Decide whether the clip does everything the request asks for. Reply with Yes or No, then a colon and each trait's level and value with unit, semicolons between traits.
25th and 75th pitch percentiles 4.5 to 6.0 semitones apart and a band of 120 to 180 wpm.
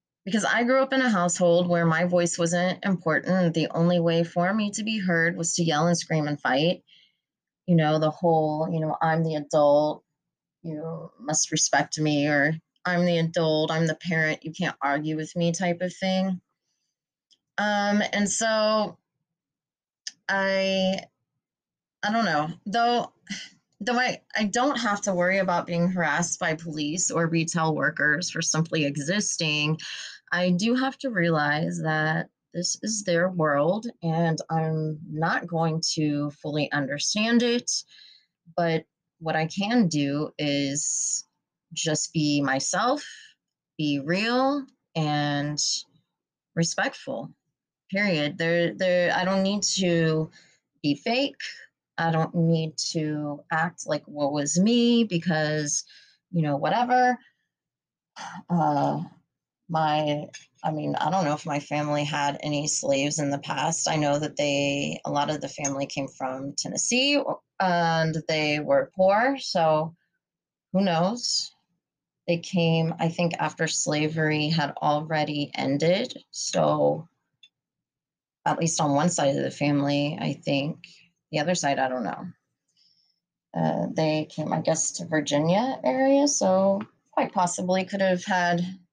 No: average, 3.7 semitones; average, 140 wpm